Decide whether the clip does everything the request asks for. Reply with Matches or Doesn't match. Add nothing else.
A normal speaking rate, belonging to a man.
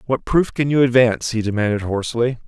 Matches